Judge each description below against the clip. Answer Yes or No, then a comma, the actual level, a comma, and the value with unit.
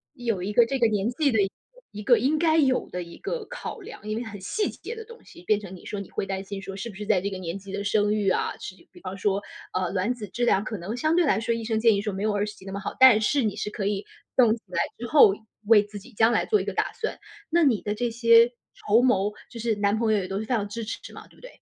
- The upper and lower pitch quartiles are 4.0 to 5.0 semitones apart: No, average, 3.4 semitones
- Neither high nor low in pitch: No, high, 215 Hz